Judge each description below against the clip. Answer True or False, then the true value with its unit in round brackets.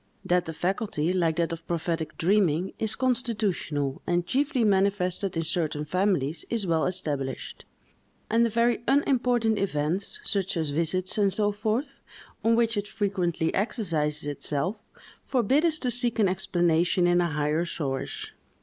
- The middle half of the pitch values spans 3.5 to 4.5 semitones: False (5.3 semitones)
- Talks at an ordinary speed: True (150 wpm)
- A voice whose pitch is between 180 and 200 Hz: True (185 Hz)